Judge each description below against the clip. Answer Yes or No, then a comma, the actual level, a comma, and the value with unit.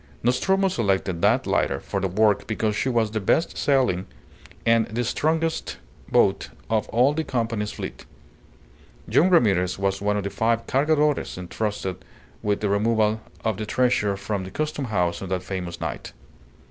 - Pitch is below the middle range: Yes, low, 110 Hz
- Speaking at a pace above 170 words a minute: No, average, 160 wpm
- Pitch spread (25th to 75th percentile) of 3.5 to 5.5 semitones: Yes, average, 4.4 semitones